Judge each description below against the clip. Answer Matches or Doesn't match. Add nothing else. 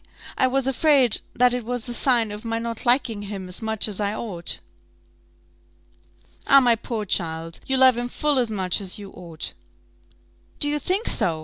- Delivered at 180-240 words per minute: Matches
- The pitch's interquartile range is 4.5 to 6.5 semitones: Doesn't match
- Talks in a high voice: Matches